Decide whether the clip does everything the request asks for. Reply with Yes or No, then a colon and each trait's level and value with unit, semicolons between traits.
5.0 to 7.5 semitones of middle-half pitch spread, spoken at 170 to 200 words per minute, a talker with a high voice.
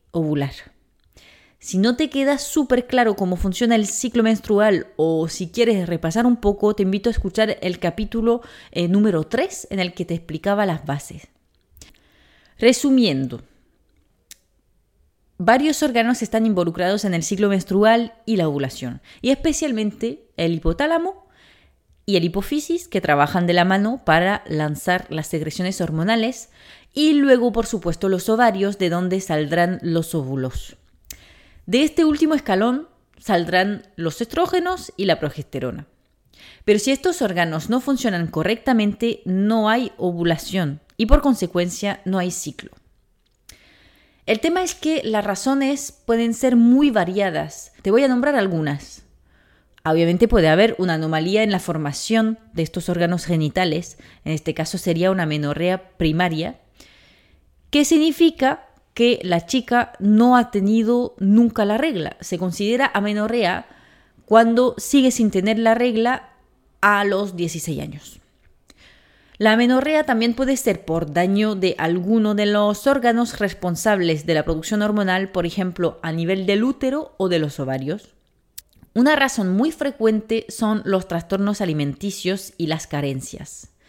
No: wide, 5.5 semitones; average, 140 wpm; high, 200 Hz